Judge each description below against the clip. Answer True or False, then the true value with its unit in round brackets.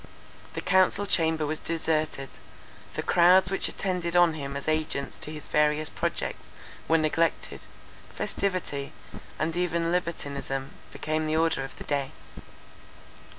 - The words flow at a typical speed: False (130 wpm)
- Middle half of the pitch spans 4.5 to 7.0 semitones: False (2.4 semitones)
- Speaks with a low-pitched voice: False (155 Hz)